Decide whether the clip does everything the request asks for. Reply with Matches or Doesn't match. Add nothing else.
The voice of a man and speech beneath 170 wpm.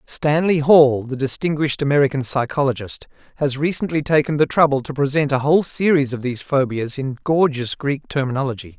Matches